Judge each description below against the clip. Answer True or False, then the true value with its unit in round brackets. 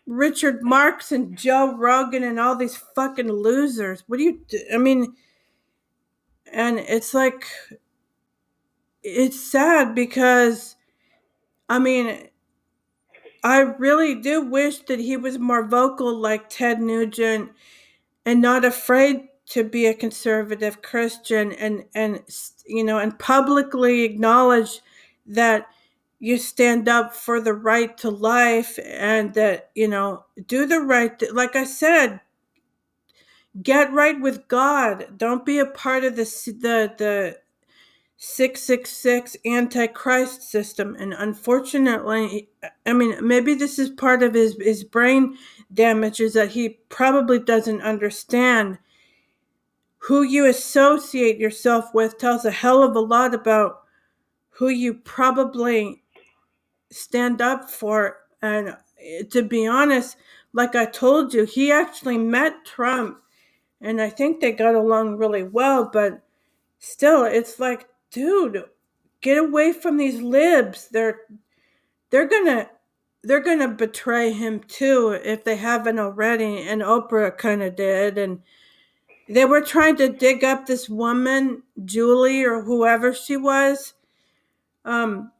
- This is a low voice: False (245 Hz)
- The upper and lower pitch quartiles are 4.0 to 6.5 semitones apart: False (3.1 semitones)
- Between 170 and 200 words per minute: False (135 wpm)